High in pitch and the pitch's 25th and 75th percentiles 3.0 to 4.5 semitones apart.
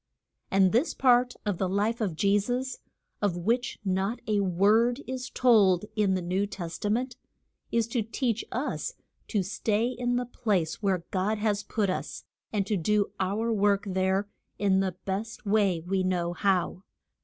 Yes: high, 205 Hz; average, 3.3 semitones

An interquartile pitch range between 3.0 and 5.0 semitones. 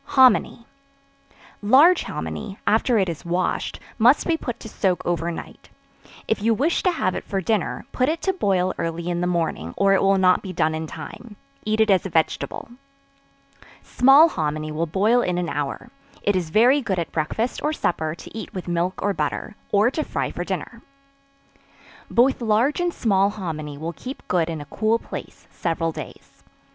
No: wide, 5.5 semitones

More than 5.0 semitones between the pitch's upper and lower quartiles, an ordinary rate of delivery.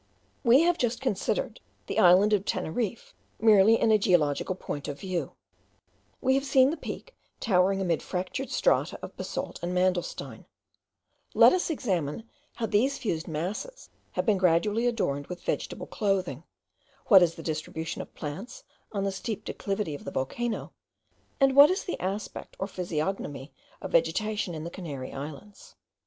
Yes: wide, 5.6 semitones; average, 155 wpm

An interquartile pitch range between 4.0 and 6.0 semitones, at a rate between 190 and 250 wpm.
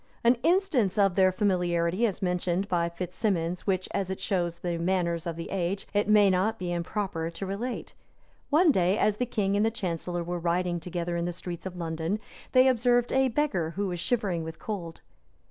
No: average, 3.5 semitones; average, 195 wpm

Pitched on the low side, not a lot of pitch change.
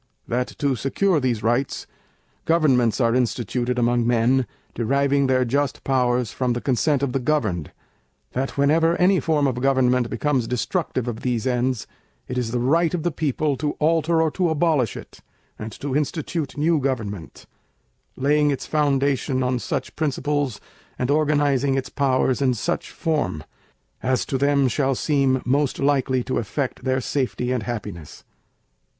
No: low, 130 Hz; average, 3.0 semitones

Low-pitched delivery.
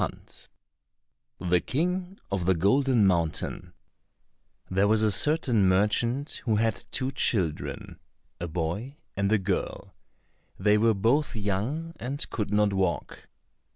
Yes: low, 105 Hz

